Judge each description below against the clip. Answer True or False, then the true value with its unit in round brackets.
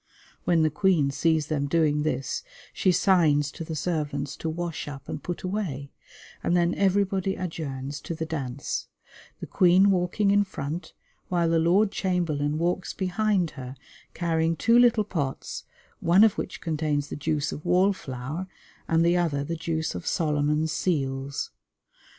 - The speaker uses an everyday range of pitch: True (3.6 semitones)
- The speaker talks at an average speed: True (155 wpm)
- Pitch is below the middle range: False (165 Hz)